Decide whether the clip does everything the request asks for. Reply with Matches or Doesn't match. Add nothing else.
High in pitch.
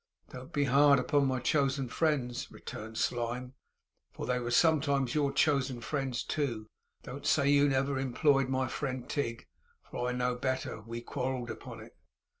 Doesn't match